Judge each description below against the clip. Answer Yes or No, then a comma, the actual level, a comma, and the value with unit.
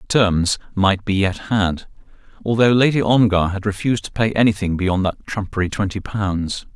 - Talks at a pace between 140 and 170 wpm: Yes, average, 160 wpm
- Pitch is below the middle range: Yes, low, 100 Hz